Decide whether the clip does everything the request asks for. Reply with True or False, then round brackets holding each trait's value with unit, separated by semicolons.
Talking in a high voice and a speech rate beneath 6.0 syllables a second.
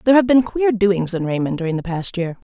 False (200 Hz; 6.1 syllables/s)